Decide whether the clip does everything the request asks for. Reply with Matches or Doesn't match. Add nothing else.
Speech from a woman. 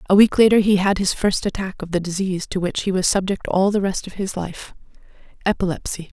Matches